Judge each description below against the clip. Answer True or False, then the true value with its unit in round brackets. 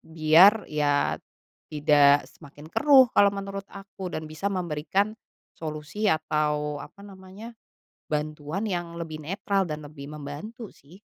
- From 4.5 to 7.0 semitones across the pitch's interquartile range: True (4.8 semitones)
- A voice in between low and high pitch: True (155 Hz)